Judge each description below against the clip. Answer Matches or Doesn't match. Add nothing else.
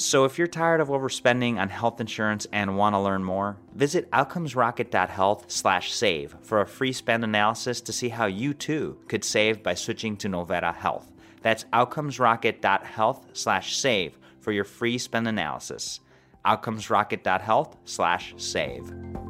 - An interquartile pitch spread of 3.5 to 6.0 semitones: Matches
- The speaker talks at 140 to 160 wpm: Matches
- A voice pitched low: Matches